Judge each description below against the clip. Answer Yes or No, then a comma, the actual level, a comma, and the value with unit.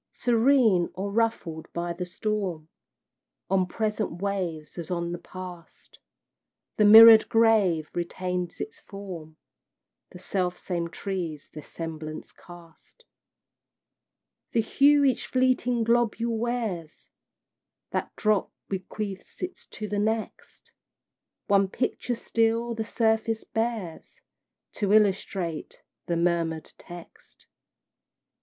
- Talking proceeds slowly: Yes, slow, 105 wpm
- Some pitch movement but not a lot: Yes, average, 4.6 semitones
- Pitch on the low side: No, high, 195 Hz